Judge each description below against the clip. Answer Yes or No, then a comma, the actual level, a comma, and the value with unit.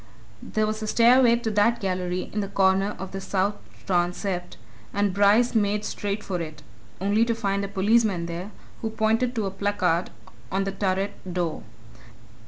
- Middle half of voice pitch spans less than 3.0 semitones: Yes, narrow, 2.5 semitones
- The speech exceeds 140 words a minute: Yes, average, 170 wpm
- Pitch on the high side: Yes, high, 200 Hz